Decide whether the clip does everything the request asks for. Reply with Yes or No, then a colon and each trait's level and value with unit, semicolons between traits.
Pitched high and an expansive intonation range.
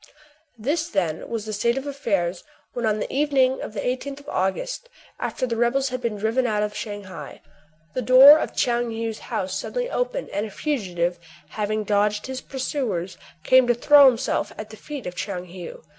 No: high, 235 Hz; average, 4.4 semitones